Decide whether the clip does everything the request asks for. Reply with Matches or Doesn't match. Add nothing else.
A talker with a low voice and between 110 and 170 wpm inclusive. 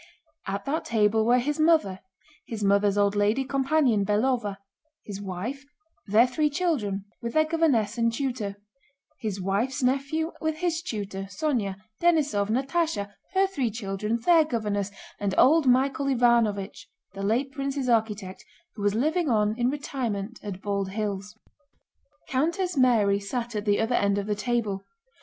Doesn't match